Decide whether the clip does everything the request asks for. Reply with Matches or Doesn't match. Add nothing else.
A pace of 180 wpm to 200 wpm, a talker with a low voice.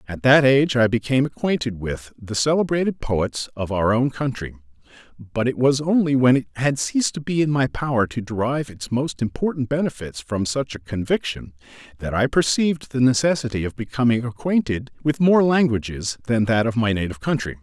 Matches